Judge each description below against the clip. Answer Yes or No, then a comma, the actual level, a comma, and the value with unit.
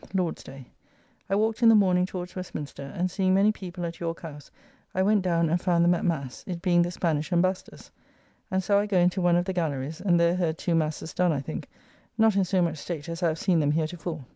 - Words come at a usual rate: No, fast, 240 wpm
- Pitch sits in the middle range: Yes, medium, 175 Hz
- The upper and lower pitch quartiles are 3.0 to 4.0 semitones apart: No, narrow, 2.4 semitones